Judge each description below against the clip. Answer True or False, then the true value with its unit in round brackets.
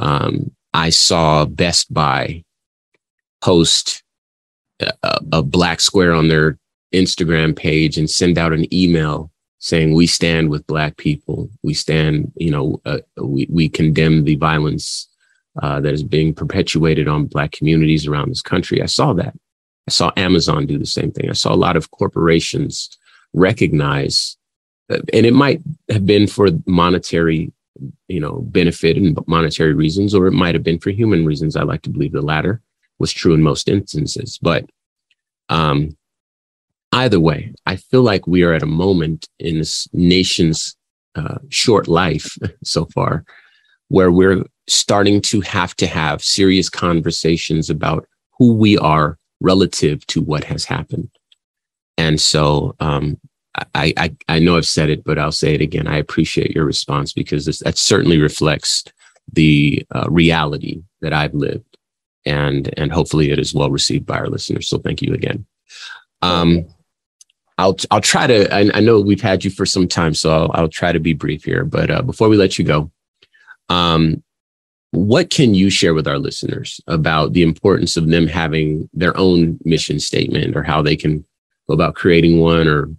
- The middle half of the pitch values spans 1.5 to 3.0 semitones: True (2.6 semitones)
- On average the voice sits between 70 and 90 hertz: True (80 Hz)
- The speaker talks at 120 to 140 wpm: False (170 wpm)